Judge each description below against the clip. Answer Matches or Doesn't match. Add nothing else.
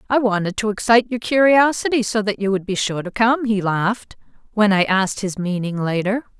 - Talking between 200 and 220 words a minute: Matches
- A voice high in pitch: Matches